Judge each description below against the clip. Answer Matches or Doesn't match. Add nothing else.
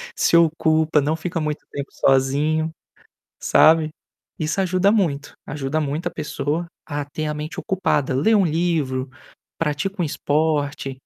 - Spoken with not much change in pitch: Matches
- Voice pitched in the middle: Matches